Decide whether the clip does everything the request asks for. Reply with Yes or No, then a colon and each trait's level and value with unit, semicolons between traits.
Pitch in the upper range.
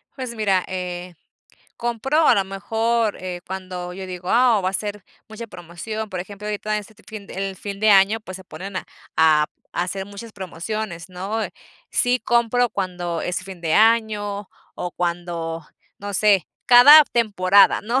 Yes: high, 200 Hz